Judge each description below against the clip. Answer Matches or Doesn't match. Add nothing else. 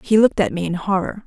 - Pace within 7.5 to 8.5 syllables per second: Doesn't match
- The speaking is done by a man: Doesn't match